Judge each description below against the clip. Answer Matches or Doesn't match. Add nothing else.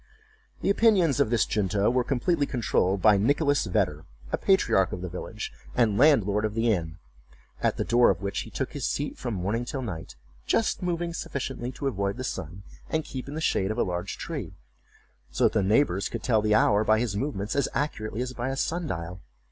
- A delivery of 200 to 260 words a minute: Matches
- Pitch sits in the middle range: Doesn't match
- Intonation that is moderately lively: Doesn't match